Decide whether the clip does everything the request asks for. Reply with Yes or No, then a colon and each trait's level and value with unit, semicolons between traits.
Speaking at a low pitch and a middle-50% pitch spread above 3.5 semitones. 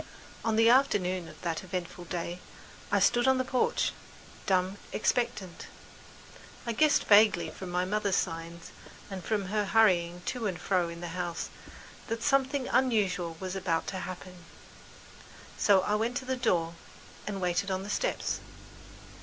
No: high, 190 Hz; average, 4.1 semitones